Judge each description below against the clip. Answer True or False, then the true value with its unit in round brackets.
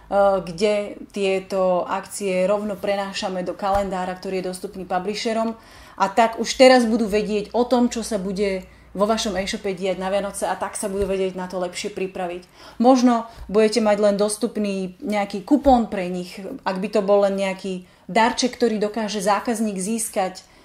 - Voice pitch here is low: False (200 Hz)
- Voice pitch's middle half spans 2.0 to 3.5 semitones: True (2.7 semitones)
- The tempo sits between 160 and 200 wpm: True (165 wpm)